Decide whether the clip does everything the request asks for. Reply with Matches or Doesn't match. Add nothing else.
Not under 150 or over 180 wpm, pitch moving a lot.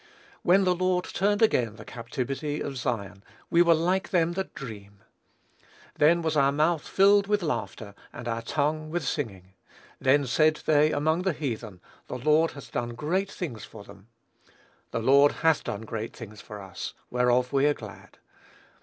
Matches